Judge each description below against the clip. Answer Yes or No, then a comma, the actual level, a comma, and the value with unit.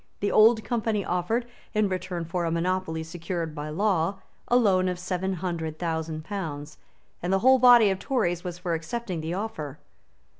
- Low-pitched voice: No, medium, 180 Hz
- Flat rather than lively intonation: No, average, 3.8 semitones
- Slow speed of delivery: No, average, 175 wpm